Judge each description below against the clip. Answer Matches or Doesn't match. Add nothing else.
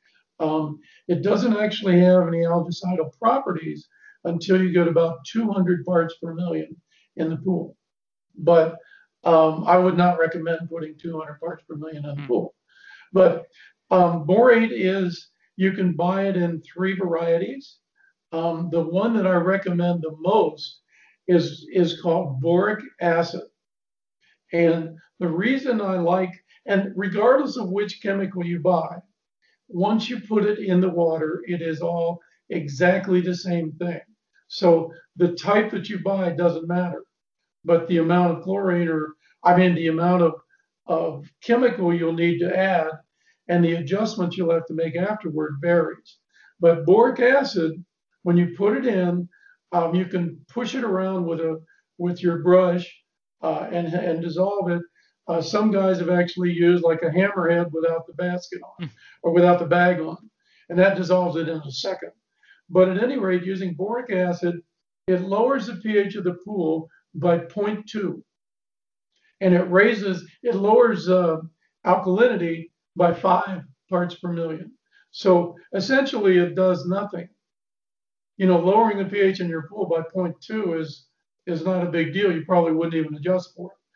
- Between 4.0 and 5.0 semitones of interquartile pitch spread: Doesn't match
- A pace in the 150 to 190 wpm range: Matches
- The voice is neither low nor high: Matches